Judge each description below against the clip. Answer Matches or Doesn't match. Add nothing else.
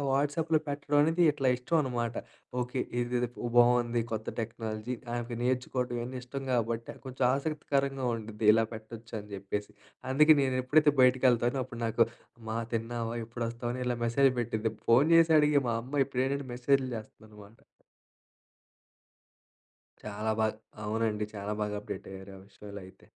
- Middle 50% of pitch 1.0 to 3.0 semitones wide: Doesn't match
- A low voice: Matches